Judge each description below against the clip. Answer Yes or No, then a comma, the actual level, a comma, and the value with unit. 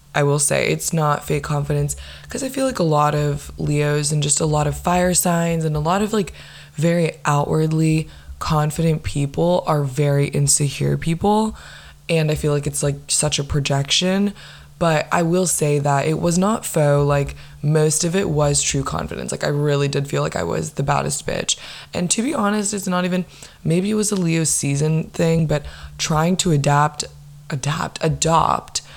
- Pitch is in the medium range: Yes, medium, 150 Hz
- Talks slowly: No, average, 190 wpm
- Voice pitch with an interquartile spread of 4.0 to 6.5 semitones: No, average, 3.0 semitones